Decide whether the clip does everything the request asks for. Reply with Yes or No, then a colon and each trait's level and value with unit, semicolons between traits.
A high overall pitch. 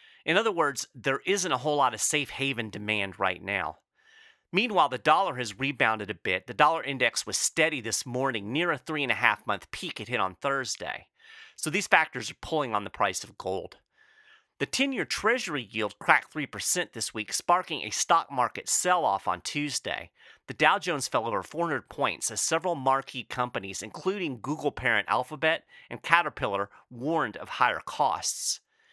No: low, 135 Hz